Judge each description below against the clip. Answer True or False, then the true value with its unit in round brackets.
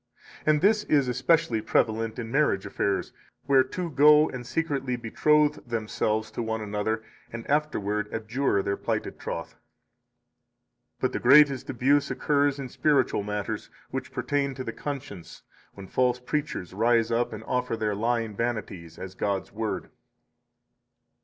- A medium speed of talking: True (145 wpm)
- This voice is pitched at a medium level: False (120 Hz)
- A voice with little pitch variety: False (4.6 semitones)